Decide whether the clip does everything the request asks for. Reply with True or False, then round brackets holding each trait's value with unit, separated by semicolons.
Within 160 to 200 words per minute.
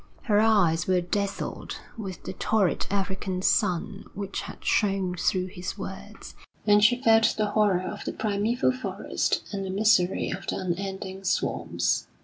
False (150 wpm)